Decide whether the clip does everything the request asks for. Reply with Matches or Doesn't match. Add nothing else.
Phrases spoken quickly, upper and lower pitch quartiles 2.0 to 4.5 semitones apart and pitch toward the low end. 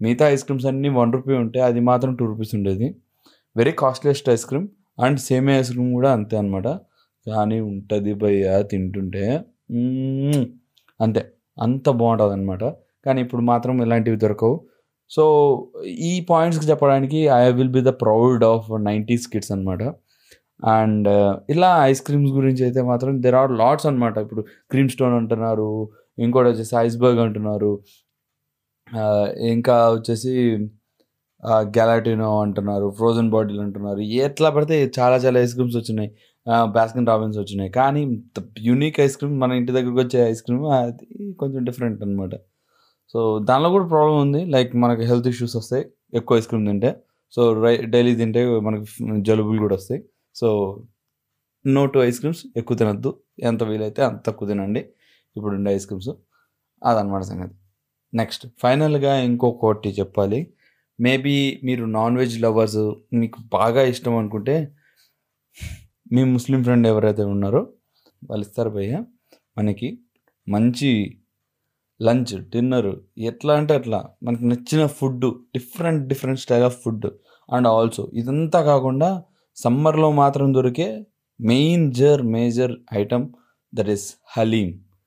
Matches